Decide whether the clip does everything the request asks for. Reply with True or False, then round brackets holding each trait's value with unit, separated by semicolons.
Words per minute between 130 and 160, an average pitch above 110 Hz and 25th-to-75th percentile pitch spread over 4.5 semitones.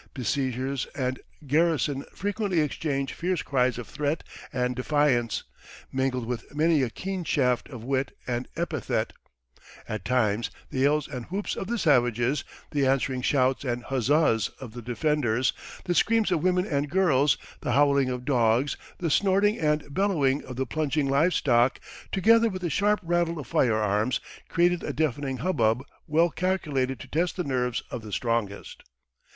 True (155 wpm; 140 Hz; 4.9 semitones)